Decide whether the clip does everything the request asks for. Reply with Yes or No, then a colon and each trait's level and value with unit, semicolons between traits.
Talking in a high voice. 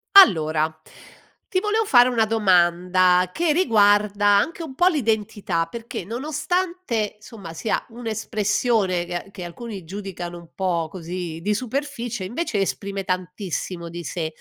Yes: high, 205 Hz